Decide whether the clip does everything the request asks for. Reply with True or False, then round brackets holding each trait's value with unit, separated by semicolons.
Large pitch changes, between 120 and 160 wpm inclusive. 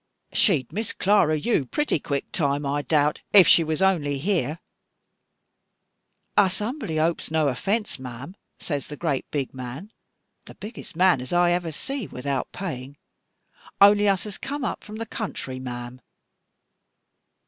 True (6.3 semitones; 150 wpm)